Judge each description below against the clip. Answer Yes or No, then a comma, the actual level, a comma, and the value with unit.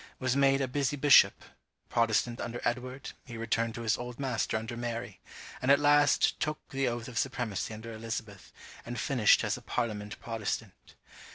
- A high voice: No, low, 120 Hz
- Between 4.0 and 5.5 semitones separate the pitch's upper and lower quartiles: No, average, 2.9 semitones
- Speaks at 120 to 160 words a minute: No, average, 170 wpm